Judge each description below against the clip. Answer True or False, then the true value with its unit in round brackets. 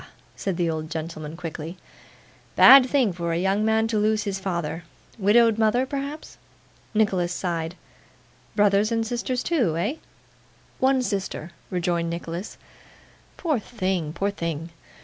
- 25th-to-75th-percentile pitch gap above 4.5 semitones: True (4.9 semitones)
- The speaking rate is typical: False (130 wpm)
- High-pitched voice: True (195 Hz)